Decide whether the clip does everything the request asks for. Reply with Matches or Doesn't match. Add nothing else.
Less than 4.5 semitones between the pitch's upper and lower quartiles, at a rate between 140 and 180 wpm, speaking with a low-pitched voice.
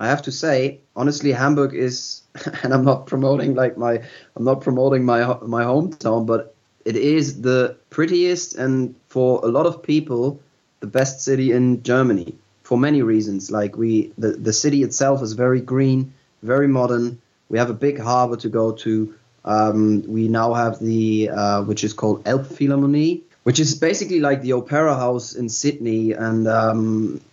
Matches